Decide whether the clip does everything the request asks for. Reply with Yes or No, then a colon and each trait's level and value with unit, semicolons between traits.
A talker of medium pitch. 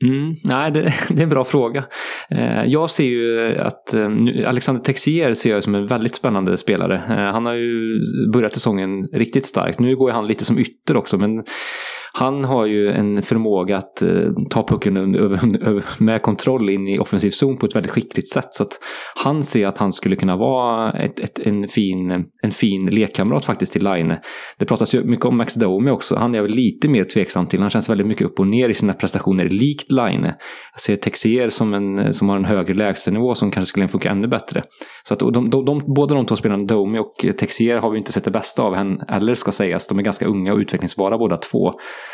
No: low, 115 Hz